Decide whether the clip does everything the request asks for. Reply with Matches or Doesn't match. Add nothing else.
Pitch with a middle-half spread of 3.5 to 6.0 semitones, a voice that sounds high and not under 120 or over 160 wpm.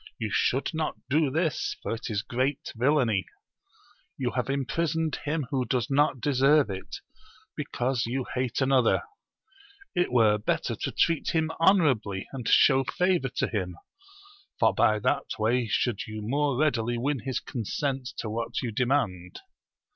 Doesn't match